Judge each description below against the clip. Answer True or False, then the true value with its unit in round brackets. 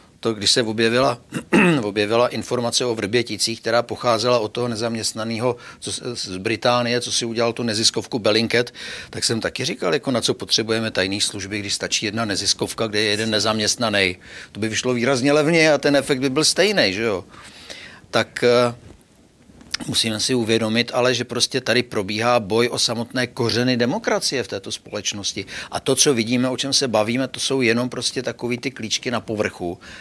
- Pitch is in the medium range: False (120 Hz)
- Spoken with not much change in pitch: True (2.1 semitones)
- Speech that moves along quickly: True (175 wpm)